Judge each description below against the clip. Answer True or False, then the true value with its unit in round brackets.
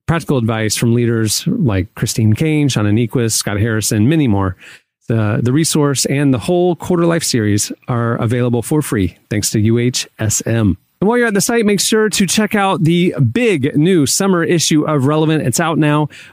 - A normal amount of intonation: False (6.7 semitones)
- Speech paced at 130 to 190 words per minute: True (185 wpm)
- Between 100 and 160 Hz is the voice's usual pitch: True (140 Hz)